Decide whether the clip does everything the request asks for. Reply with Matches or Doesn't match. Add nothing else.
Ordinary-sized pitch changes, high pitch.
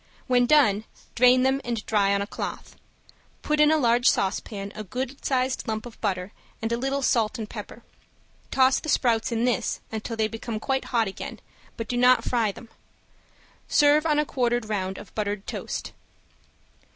Matches